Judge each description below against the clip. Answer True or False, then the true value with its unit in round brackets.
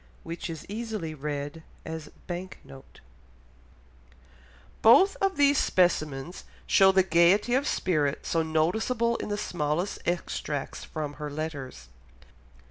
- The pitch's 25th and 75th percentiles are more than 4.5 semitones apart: True (5.5 semitones)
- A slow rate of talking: True (120 wpm)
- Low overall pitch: False (170 Hz)